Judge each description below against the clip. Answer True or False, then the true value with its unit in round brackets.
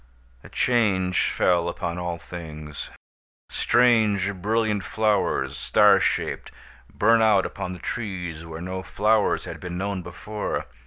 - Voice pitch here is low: True (95 Hz)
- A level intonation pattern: False (3.6 semitones)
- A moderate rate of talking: False (125 wpm)